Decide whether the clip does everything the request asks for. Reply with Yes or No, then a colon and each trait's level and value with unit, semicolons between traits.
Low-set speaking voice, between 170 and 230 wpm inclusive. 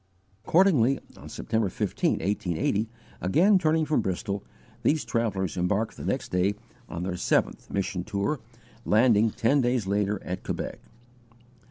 No: low, 105 Hz; slow, 135 wpm